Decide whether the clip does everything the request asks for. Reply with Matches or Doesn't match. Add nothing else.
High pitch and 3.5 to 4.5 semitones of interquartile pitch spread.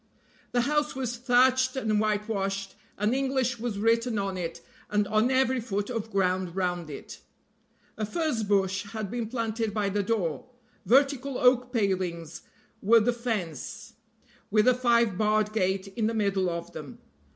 Matches